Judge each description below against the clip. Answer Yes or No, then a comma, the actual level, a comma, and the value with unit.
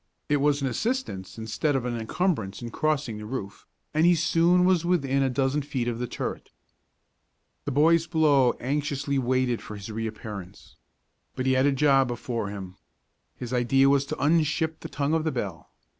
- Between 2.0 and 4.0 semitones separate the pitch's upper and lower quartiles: No, average, 4.4 semitones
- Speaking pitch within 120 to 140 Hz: Yes, low, 135 Hz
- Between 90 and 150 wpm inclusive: No, average, 180 wpm